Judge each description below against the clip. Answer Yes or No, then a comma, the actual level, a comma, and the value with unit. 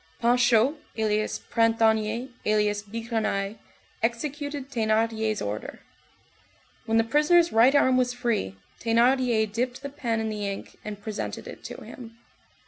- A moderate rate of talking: No, slow, 130 wpm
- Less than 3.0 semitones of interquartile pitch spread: Yes, narrow, 2.5 semitones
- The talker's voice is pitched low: No, high, 230 Hz